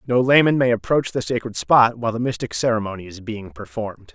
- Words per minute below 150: No, fast, 205 wpm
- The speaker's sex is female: No, male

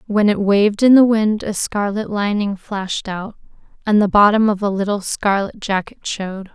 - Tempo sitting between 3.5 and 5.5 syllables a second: Yes, 4.9 syllables/s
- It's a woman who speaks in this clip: Yes, female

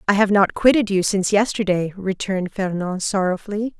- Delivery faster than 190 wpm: No, average, 160 wpm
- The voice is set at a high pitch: Yes, high, 195 Hz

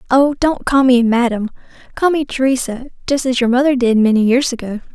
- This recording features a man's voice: No, female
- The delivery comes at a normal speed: Yes, average, 195 wpm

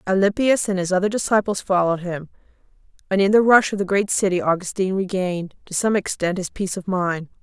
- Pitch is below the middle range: No, high, 190 Hz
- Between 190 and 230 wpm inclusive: Yes, average, 195 wpm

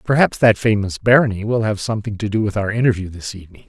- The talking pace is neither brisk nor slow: No, fast, 230 wpm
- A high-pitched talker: No, low, 105 Hz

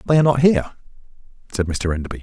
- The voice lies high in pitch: No, low, 115 Hz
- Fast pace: No, average, 190 wpm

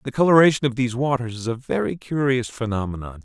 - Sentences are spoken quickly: No, average, 185 wpm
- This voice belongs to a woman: No, male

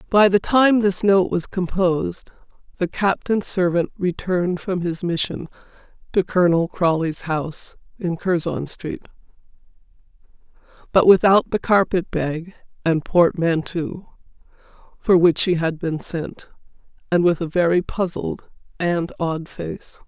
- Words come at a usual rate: No, slow, 125 wpm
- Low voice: No, medium, 175 Hz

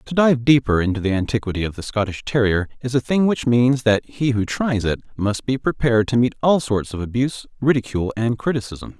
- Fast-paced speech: Yes, fast, 215 wpm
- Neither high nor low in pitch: No, low, 120 Hz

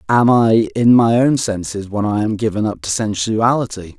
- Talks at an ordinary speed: Yes, average, 195 wpm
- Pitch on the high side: No, low, 110 Hz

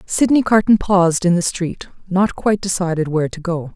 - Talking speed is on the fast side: No, average, 190 wpm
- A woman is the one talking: Yes, female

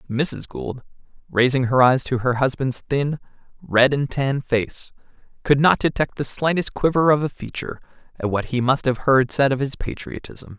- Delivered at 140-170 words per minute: No, average, 180 wpm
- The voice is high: No, low, 135 Hz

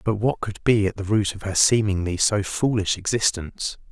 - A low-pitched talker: Yes, low, 100 Hz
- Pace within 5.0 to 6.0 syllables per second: Yes, 5.2 syllables/s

